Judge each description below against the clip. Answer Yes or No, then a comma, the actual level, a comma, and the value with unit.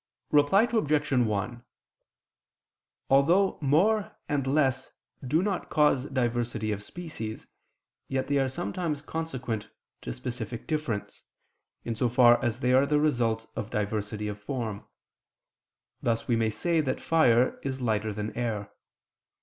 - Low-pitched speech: Yes, low, 125 Hz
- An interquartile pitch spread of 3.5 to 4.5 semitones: No, average, 5.0 semitones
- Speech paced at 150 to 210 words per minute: No, slow, 135 wpm